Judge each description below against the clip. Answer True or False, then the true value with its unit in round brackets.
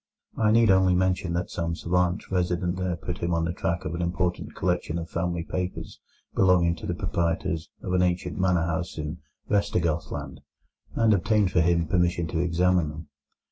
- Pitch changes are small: True (1.5 semitones)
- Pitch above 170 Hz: False (90 Hz)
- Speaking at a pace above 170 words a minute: True (180 wpm)